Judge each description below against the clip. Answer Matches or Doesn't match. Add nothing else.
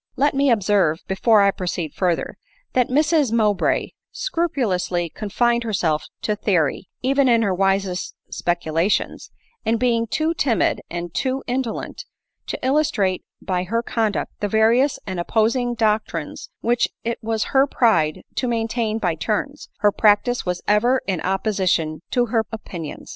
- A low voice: Doesn't match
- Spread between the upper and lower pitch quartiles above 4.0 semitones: Matches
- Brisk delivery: Doesn't match